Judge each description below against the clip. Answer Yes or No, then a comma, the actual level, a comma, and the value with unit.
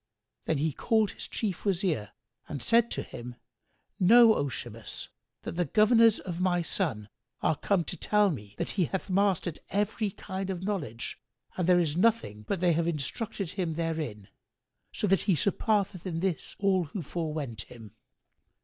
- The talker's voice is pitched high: No, medium, 180 Hz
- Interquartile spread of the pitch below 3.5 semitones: No, average, 4.8 semitones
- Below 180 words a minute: Yes, average, 165 wpm